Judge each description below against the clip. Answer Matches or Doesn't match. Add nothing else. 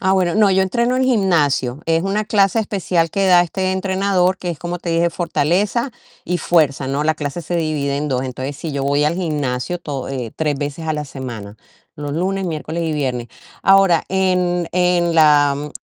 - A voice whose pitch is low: Doesn't match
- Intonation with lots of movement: Doesn't match